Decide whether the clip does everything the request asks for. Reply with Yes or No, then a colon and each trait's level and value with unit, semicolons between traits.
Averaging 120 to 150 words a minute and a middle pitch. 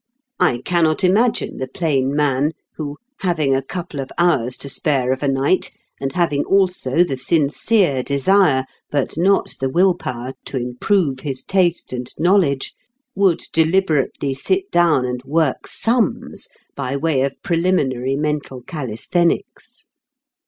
Yes: average, 140 wpm; medium, 145 Hz